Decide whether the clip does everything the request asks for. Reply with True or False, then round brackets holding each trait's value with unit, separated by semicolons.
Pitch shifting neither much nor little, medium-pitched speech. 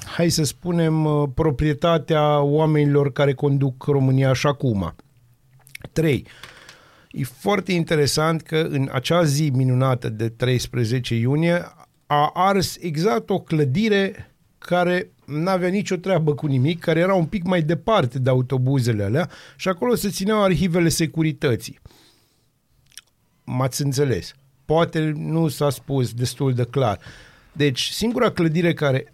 True (4.4 semitones; 150 Hz)